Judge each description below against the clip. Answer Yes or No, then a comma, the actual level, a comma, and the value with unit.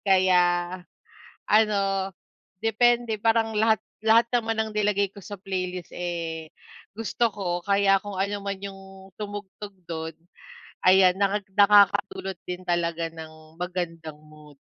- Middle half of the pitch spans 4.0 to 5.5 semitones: No, average, 2.9 semitones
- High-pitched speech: Yes, high, 195 Hz